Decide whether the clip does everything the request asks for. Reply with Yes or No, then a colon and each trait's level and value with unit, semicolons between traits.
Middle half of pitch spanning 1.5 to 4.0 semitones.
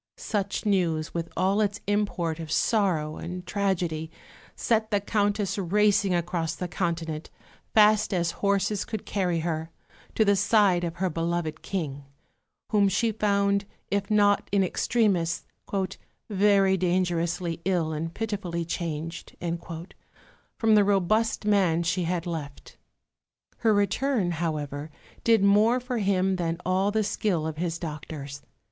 Yes: average, 3.5 semitones